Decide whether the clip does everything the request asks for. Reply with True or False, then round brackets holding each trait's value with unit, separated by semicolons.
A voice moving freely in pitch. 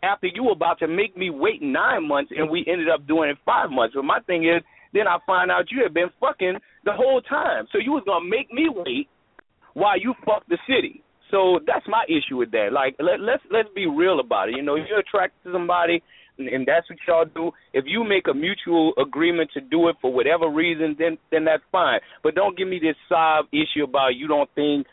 True (6.6 semitones)